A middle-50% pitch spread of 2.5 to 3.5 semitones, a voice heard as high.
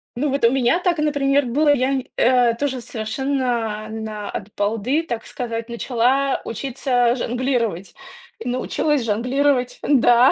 Yes: average, 3.0 semitones; very high, 250 Hz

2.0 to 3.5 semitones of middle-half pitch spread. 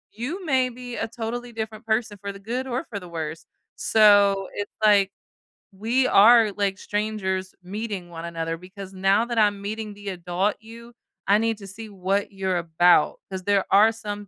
Yes: average, 2.8 semitones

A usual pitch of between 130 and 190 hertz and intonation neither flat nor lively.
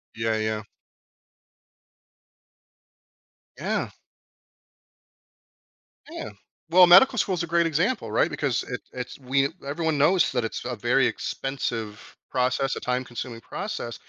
No: low, 135 Hz; wide, 6.0 semitones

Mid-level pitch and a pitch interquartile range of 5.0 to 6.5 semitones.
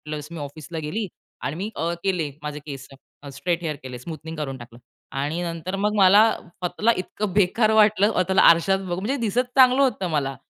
Yes: medium, 175 Hz; average, 5.3 semitones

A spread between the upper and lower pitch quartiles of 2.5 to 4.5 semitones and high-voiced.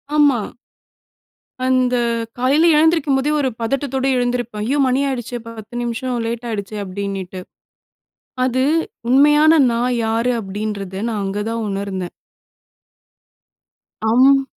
Yes: average, 4.2 semitones; high, 240 Hz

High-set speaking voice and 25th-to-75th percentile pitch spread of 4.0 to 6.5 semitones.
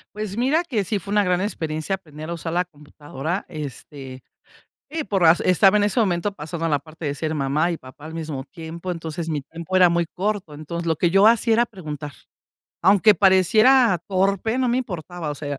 No: medium, 175 Hz; average, 4.5 semitones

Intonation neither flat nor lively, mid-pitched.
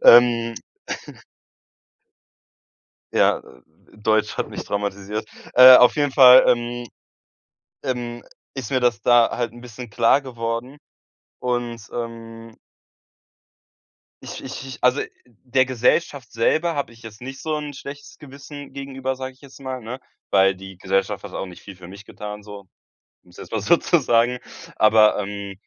No: average, 3.4 semitones; low, 120 Hz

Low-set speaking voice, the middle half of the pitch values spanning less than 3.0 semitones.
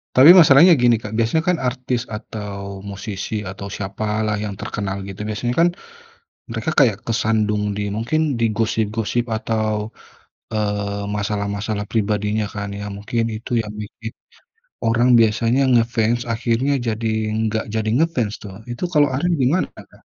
Yes: low, 110 Hz; narrow, 2.5 semitones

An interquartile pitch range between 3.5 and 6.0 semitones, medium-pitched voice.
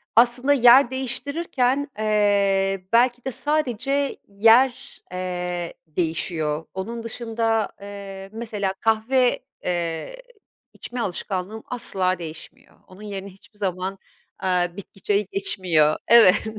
No: average, 4.6 semitones; high, 205 Hz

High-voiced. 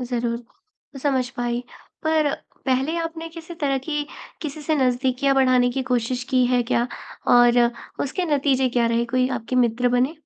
Yes: very high, 255 Hz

